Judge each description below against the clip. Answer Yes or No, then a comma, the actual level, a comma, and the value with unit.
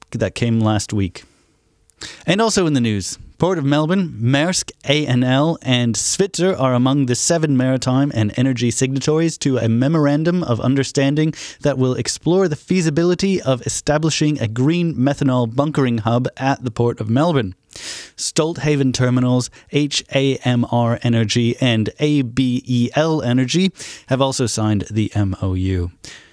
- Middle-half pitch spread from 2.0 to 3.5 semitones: No, average, 4.0 semitones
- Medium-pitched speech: No, low, 130 Hz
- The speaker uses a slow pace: Yes, slow, 130 wpm